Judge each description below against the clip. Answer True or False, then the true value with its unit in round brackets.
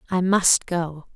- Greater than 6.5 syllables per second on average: False (3.4 syllables/s)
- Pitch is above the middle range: False (175 Hz)